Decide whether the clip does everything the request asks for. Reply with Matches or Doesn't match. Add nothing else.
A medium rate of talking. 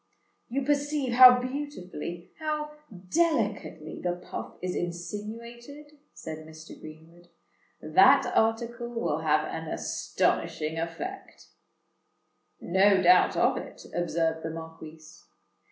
Doesn't match